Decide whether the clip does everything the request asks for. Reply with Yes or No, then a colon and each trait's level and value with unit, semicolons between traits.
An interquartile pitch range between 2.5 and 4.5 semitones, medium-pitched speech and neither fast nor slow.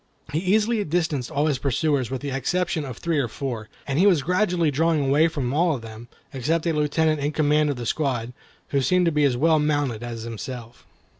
No: average, 4.1 semitones; medium, 145 Hz; fast, 215 wpm